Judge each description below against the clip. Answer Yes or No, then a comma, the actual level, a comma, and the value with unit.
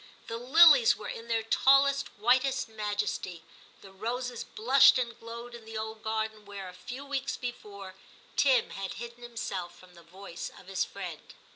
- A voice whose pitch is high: Yes, high, 225 Hz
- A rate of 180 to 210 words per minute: No, average, 165 wpm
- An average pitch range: Yes, average, 4.0 semitones